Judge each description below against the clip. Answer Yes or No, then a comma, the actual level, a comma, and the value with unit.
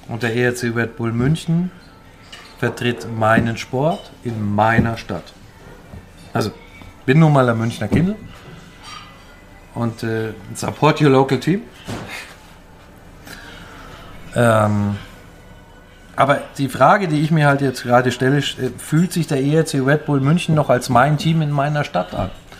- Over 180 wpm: No, average, 135 wpm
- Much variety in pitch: Yes, wide, 6.1 semitones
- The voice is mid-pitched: No, low, 120 Hz